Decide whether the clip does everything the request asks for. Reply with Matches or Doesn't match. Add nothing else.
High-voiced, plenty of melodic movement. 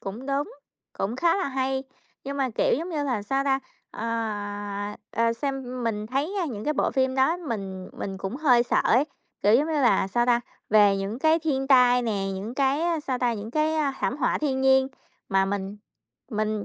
Doesn't match